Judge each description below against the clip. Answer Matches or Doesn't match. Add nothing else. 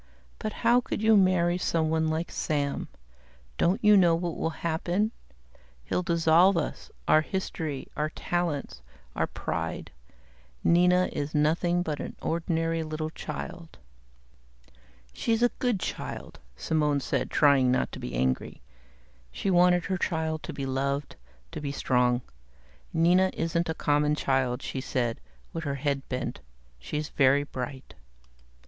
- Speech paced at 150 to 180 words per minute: Doesn't match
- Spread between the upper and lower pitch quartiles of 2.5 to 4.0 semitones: Matches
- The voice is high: Doesn't match